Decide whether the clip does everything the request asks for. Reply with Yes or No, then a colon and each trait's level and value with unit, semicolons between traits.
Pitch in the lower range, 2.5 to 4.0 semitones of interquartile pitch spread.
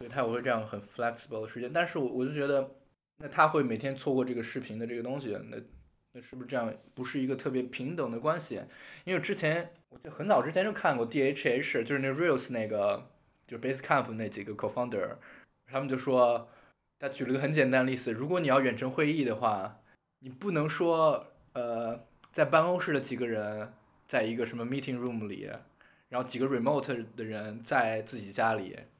Yes: low, 130 Hz; average, 3.2 semitones